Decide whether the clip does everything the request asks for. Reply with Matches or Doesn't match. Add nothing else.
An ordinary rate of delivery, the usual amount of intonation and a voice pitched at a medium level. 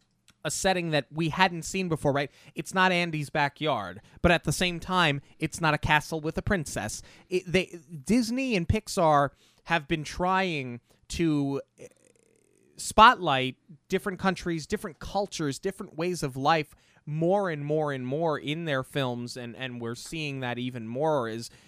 Matches